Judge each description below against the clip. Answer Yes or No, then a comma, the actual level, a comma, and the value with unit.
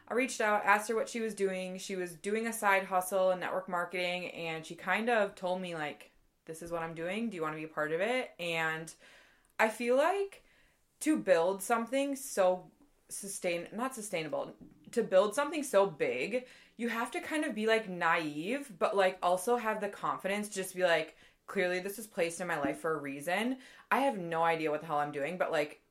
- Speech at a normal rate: No, fast, 220 wpm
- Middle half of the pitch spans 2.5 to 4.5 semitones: No, average, 5.3 semitones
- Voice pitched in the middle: No, high, 195 Hz